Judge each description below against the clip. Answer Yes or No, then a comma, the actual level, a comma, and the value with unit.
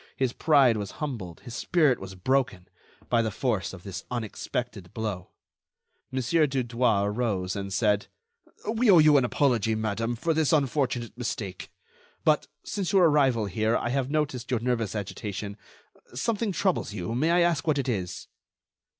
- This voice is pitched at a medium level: No, low, 120 Hz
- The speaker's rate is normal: Yes, average, 160 wpm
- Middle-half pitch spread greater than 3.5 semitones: Yes, wide, 5.6 semitones